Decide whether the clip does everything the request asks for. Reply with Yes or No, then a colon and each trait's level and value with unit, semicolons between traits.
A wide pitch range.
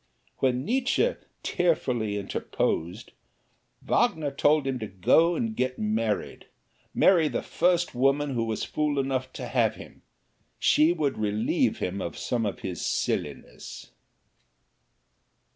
Yes: wide, 6.2 semitones